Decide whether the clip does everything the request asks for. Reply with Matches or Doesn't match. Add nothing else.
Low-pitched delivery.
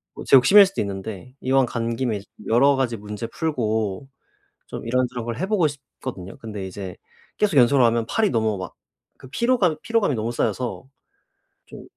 Matches